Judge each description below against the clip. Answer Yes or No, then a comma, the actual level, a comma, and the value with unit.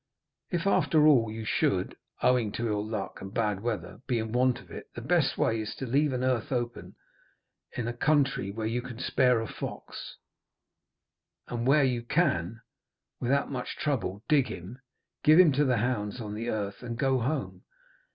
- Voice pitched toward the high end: No, low, 120 Hz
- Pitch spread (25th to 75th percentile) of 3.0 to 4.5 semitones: Yes, average, 3.4 semitones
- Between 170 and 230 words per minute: Yes, average, 180 wpm